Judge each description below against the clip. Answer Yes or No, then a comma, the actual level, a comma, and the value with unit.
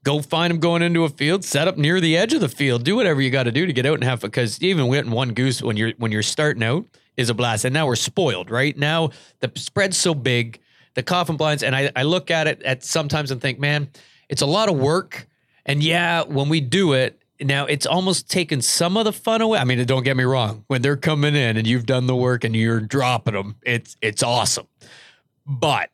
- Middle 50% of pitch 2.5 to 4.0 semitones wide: No, average, 4.4 semitones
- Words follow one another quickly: Yes, fast, 245 wpm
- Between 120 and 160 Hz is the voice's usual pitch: Yes, medium, 140 Hz